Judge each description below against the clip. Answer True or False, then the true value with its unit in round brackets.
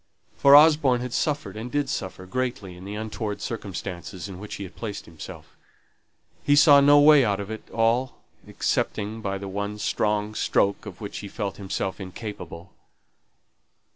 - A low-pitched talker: True (105 Hz)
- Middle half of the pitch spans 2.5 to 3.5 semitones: False (4.2 semitones)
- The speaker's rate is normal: True (165 wpm)